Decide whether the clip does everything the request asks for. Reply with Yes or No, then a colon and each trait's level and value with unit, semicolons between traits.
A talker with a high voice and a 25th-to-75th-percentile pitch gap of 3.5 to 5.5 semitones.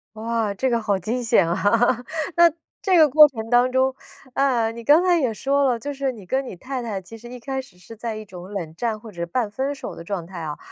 Yes: high, 235 Hz; average, 4.5 semitones